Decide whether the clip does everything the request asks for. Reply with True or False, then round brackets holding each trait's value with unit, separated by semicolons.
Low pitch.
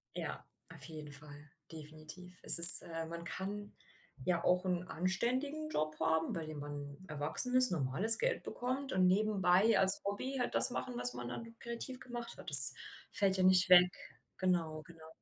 False (180 Hz)